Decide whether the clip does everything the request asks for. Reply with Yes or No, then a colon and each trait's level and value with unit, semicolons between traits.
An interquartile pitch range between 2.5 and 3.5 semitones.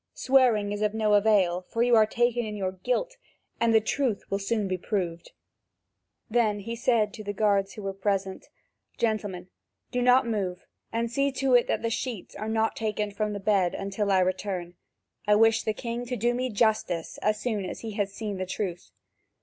Yes: average, 2.9 semitones